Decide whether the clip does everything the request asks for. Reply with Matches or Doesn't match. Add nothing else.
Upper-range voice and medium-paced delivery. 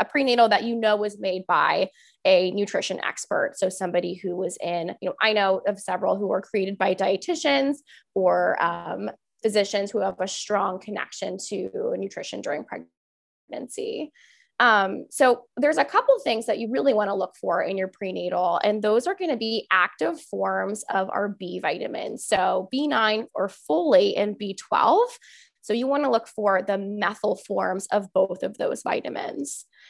Matches